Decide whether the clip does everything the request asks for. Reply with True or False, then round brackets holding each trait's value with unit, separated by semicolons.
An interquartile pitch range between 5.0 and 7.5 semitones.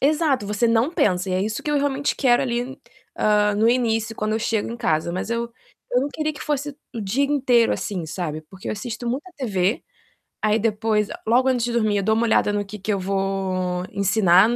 False (3.8 semitones)